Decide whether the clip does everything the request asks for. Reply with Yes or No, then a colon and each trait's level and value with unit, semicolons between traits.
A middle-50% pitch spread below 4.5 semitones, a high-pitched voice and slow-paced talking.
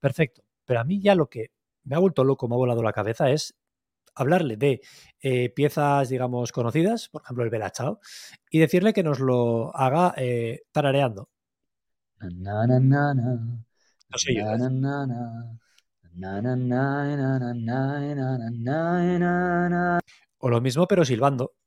No: average, 3.9 semitones; low, 130 Hz; slow, 120 wpm